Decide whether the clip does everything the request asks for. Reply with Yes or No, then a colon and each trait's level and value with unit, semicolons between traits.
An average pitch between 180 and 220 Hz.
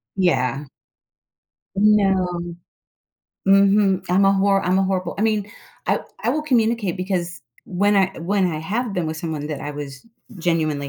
Yes: medium, 185 Hz